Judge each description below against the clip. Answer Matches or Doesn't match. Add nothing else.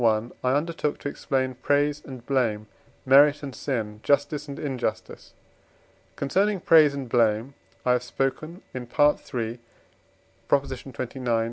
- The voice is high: Doesn't match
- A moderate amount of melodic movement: Matches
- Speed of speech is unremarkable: Doesn't match